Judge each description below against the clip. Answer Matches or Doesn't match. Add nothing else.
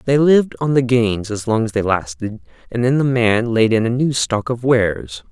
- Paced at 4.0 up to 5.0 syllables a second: Matches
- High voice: Doesn't match